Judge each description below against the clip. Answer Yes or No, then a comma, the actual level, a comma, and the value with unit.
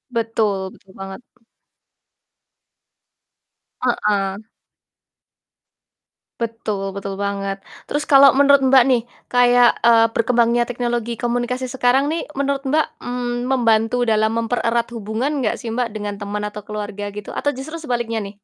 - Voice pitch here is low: No, high, 235 Hz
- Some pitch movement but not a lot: Yes, average, 3.1 semitones